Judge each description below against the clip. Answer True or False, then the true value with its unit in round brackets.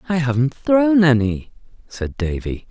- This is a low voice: True (130 Hz)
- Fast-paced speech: False (135 wpm)